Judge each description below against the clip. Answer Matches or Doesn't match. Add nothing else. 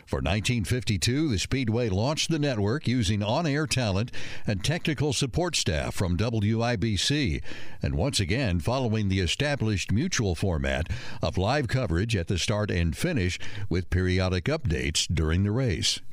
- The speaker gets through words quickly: Doesn't match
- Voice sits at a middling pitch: Doesn't match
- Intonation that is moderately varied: Doesn't match